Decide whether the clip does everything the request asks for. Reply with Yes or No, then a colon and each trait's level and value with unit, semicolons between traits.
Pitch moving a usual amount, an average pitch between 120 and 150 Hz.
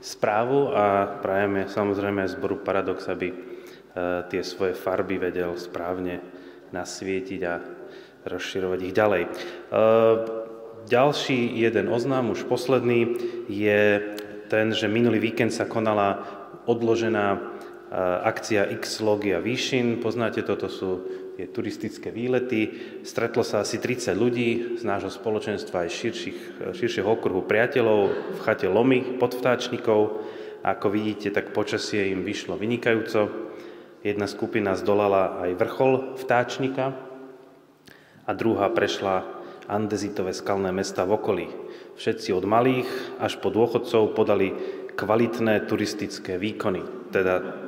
No: average, 3.7 semitones; low, 110 Hz